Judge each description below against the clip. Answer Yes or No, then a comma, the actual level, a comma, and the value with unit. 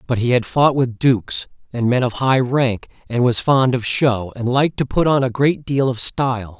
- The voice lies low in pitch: Yes, low, 125 Hz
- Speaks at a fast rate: Yes, fast, 235 wpm